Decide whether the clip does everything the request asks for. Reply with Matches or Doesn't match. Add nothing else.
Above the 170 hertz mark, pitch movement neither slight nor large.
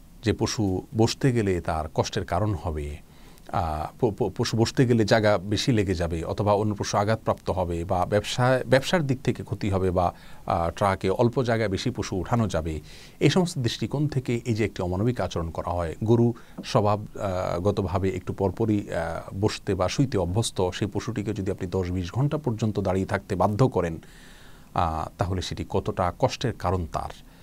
Doesn't match